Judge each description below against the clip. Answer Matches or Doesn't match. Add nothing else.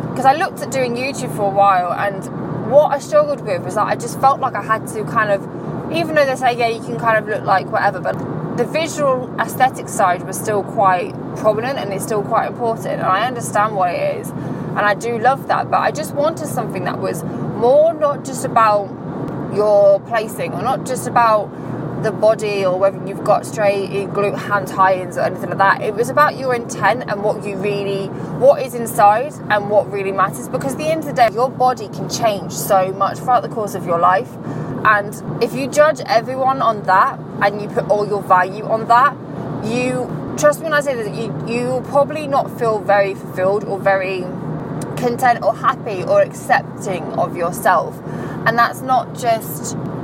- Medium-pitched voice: Doesn't match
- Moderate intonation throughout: Matches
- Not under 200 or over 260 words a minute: Matches